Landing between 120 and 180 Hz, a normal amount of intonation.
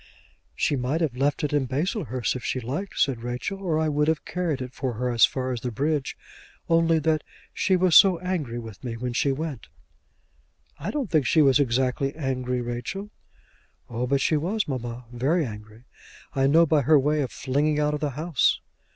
Yes: medium, 140 Hz; average, 4.1 semitones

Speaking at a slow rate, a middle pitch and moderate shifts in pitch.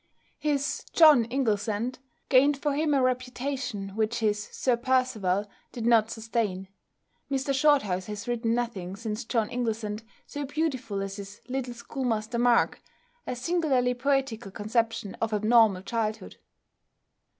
No: slow, 130 wpm; high, 235 Hz; average, 3.5 semitones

